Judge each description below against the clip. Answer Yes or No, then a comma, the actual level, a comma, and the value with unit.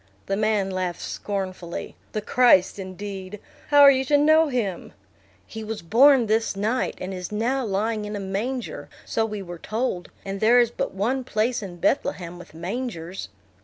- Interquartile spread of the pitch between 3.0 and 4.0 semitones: No, average, 4.4 semitones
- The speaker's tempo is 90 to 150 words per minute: No, average, 170 wpm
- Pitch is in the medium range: No, high, 210 Hz